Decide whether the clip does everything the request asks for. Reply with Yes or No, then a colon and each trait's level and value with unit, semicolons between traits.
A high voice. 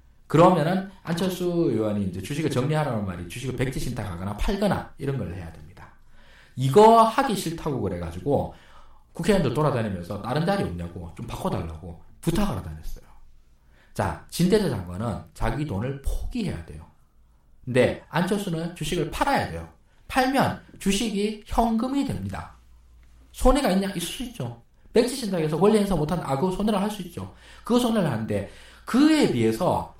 No: low, 135 Hz